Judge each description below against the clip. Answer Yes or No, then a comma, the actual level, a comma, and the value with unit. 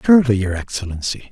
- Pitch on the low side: Yes, low, 115 Hz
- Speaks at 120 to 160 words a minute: Yes, slow, 135 wpm